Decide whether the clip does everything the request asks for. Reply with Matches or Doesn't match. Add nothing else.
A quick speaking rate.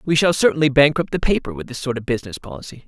Matches